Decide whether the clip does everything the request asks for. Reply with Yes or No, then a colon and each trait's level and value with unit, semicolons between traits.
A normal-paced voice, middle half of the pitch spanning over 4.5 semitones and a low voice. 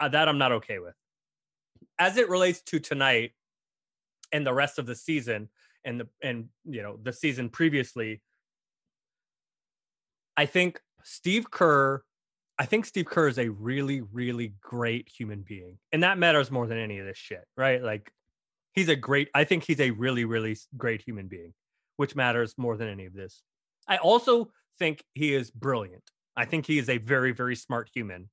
Yes: average, 180 wpm; average, 4.9 semitones; low, 130 Hz